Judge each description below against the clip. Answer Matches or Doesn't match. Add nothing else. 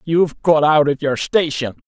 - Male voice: Matches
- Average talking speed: Matches